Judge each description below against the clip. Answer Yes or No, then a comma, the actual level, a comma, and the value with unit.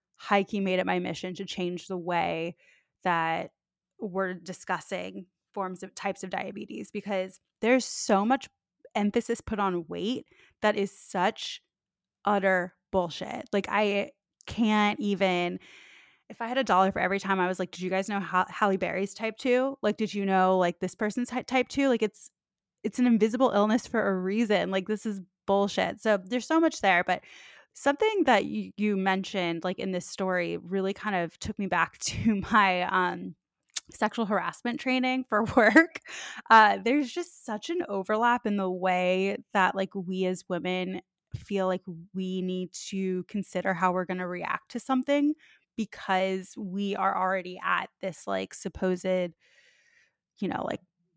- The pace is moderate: Yes, average, 170 wpm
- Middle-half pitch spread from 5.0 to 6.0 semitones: No, average, 3.0 semitones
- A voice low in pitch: No, high, 195 Hz